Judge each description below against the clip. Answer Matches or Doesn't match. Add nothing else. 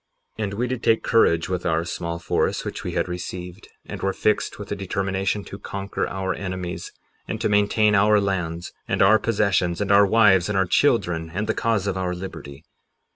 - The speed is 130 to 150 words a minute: Doesn't match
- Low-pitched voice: Matches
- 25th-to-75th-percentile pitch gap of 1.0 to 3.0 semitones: Matches